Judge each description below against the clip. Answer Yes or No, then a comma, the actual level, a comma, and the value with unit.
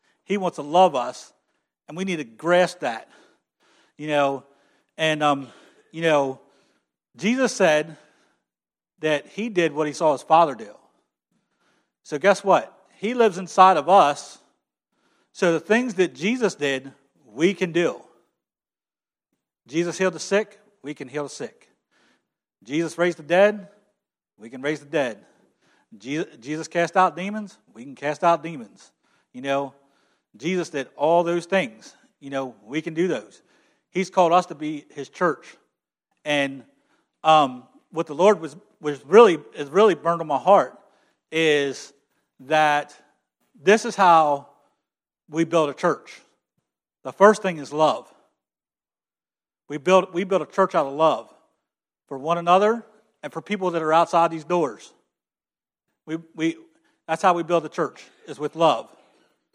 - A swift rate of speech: No, average, 150 wpm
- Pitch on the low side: No, medium, 165 Hz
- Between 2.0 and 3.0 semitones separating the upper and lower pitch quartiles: No, average, 4.3 semitones